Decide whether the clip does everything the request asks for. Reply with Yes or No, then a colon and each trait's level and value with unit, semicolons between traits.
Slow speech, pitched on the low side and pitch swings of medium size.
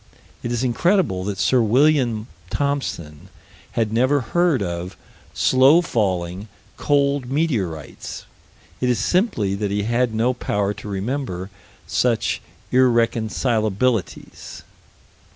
Yes: slow, 105 wpm; low, 115 Hz; average, 4.8 semitones